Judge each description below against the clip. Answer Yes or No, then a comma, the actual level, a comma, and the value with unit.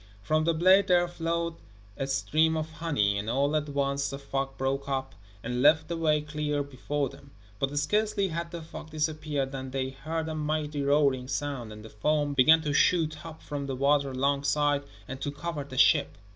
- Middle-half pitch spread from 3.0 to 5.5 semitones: No, narrow, 2.4 semitones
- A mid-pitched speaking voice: Yes, medium, 145 Hz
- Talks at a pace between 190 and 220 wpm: Yes, average, 195 wpm